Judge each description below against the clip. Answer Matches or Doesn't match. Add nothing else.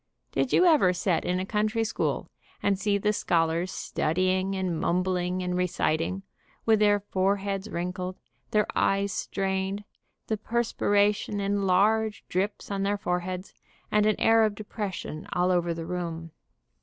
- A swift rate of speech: Doesn't match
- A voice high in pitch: Matches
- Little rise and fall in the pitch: Matches